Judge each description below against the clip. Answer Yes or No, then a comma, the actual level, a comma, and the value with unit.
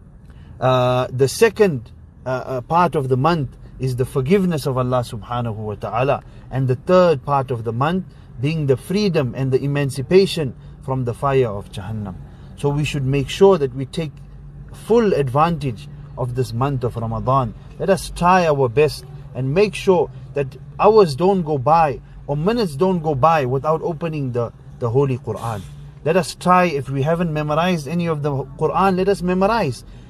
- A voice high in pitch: No, medium, 140 Hz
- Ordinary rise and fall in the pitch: Yes, average, 4.2 semitones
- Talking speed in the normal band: Yes, average, 175 wpm